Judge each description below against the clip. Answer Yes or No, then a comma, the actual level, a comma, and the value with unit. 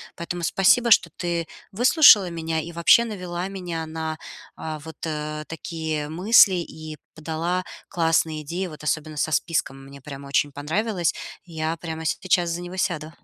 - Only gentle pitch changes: Yes, narrow, 2.3 semitones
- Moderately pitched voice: Yes, medium, 165 Hz